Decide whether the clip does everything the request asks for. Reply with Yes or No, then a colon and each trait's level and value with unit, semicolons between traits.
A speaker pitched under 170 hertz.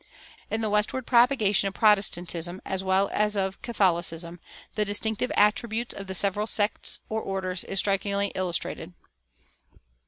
No: high, 200 Hz